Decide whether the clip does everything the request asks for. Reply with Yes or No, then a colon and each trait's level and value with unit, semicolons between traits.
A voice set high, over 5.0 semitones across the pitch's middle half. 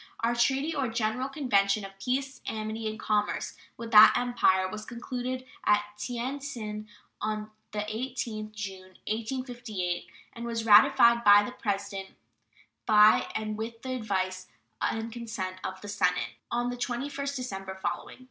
No: high, 220 Hz; average, 3.1 semitones